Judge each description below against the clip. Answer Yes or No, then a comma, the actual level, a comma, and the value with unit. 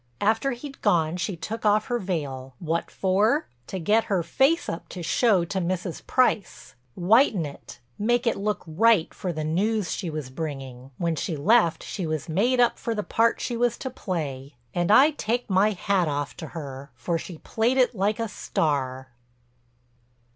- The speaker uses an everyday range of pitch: No, wide, 6.3 semitones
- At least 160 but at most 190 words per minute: Yes, average, 175 wpm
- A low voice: No, medium, 185 Hz